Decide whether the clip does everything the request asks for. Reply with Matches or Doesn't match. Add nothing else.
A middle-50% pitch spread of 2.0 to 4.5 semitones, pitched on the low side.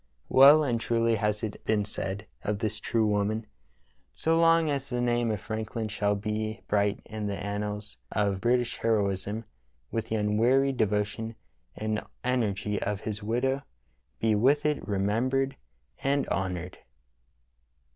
Matches